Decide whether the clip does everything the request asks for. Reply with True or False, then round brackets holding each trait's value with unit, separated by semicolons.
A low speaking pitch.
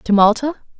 False (240 Hz)